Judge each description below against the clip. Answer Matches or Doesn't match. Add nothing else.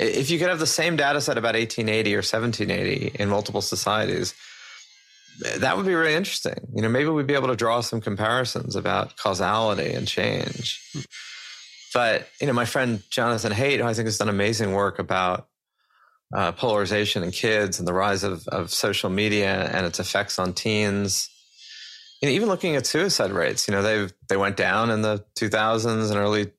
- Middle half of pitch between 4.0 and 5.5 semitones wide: Doesn't match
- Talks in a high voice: Doesn't match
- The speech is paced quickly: Doesn't match